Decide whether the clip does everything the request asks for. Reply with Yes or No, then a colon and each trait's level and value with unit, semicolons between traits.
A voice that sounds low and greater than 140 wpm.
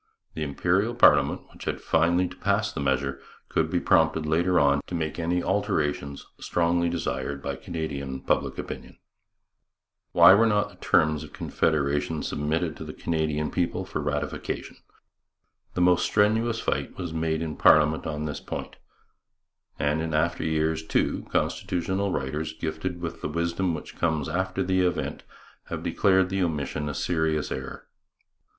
Yes: very low, 80 Hz; average, 155 wpm